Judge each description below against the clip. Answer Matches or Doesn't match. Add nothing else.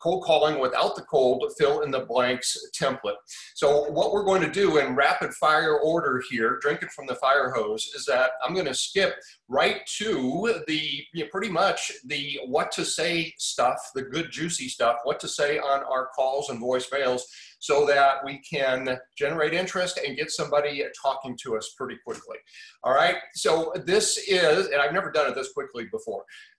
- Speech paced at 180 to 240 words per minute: Matches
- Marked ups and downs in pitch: Matches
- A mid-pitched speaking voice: Matches